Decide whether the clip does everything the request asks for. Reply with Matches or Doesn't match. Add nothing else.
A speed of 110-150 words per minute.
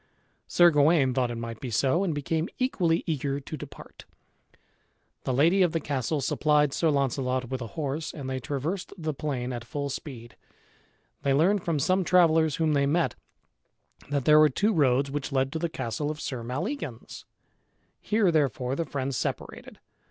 Doesn't match